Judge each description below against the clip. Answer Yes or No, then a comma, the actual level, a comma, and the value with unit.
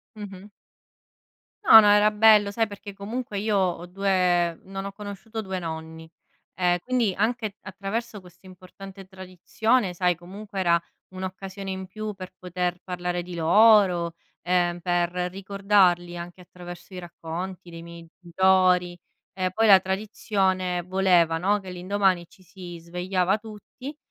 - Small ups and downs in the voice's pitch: Yes, narrow, 2.3 semitones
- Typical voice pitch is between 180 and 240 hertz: Yes, medium, 185 Hz